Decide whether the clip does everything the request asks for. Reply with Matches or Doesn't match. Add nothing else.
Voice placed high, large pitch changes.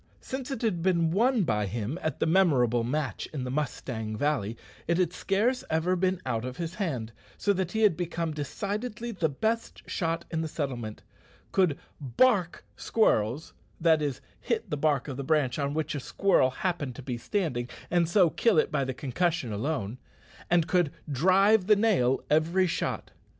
Doesn't match